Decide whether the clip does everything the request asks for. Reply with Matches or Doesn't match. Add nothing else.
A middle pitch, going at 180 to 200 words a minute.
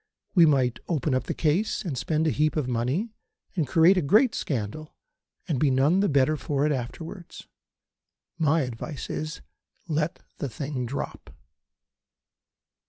Doesn't match